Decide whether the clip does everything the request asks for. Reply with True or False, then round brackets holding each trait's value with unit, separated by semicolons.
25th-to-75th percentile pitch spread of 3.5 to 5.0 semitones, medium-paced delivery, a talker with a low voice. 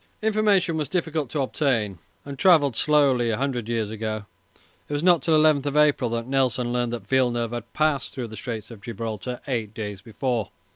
True (4.5 semitones; 185 wpm; 125 Hz)